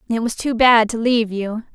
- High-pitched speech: Yes, high, 225 Hz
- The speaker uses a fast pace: Yes, fast, 240 wpm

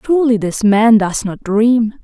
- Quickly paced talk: No, average, 175 wpm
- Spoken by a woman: Yes, female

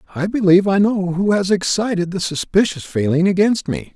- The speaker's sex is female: No, male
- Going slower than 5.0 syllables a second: No, 5.5 syllables/s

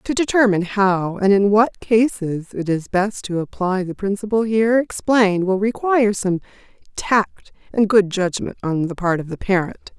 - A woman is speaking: Yes, female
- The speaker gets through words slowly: No, average, 175 wpm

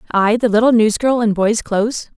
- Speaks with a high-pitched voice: Yes, high, 220 Hz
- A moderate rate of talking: Yes, average, 190 wpm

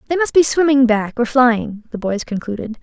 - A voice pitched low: No, high, 245 Hz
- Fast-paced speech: Yes, fast, 210 wpm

